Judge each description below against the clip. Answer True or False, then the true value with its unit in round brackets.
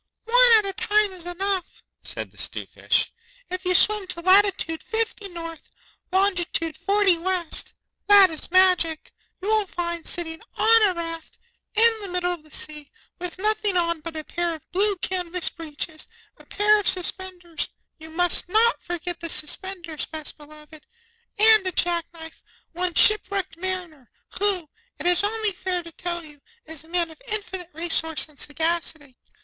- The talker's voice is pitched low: False (355 Hz)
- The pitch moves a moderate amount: True (3.2 semitones)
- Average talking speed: True (165 wpm)